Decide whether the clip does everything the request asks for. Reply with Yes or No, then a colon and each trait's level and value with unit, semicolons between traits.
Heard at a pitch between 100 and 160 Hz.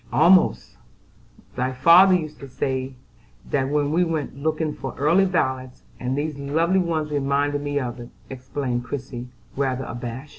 Yes: medium, 140 Hz